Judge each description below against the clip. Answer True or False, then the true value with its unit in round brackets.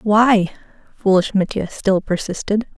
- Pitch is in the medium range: False (200 Hz)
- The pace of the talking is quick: False (110 wpm)